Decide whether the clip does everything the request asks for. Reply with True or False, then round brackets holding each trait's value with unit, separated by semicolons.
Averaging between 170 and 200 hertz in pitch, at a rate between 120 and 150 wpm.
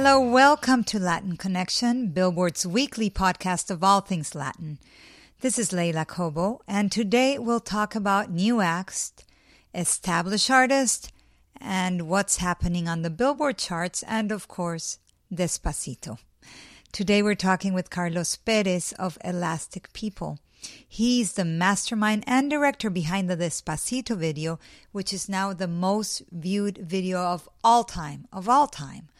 True (190 Hz; 140 wpm)